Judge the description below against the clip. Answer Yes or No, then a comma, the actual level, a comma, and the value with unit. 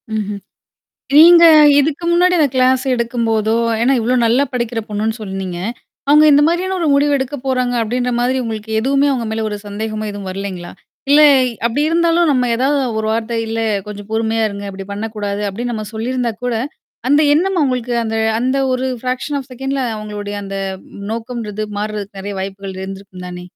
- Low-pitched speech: No, high, 230 Hz